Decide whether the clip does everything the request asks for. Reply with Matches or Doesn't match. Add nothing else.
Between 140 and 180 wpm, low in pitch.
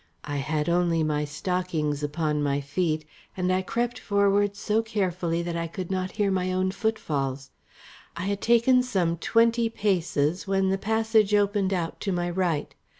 Doesn't match